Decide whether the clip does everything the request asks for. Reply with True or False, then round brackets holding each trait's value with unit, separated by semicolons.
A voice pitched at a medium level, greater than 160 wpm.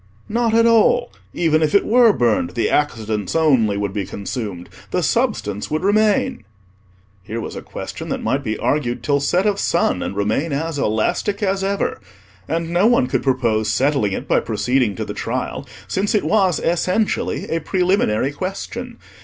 True (150 Hz; 170 wpm)